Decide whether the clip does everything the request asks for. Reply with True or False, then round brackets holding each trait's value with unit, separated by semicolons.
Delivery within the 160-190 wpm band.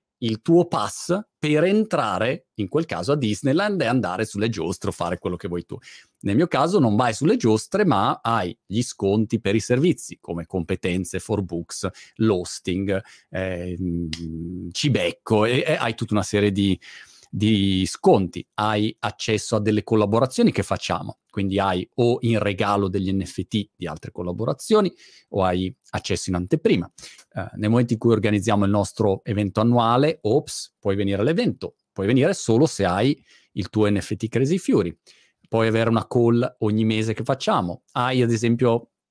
True (165 wpm)